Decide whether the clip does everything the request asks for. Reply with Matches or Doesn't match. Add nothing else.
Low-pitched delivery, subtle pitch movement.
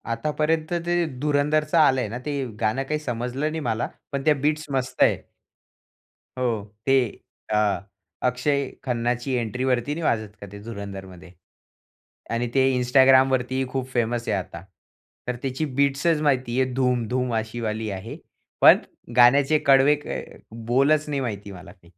Doesn't match